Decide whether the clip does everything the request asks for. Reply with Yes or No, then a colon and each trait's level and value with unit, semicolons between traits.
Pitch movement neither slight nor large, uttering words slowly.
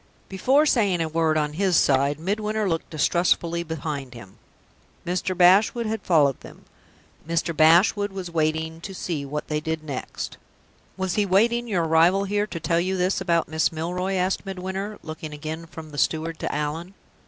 No: average, 3.4 semitones; average, 170 wpm